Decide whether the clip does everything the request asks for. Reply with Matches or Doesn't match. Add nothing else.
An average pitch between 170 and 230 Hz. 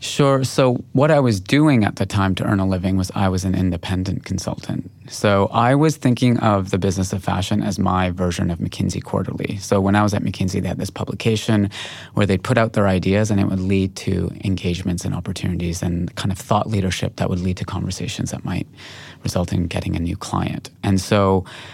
Doesn't match